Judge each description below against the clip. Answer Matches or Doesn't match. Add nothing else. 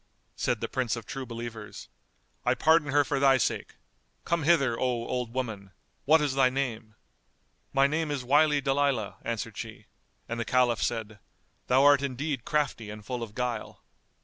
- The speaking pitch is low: Matches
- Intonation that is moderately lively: Matches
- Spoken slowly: Doesn't match